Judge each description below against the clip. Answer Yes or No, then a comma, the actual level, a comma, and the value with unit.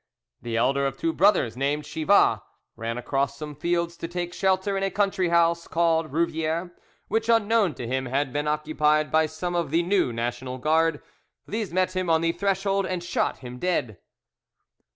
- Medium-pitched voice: Yes, medium, 165 Hz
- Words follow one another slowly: No, average, 175 wpm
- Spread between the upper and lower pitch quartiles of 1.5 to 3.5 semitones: No, average, 4.7 semitones